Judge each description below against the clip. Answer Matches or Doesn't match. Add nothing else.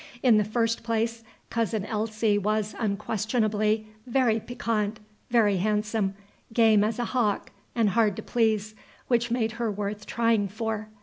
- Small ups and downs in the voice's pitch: Matches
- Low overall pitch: Doesn't match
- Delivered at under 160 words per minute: Matches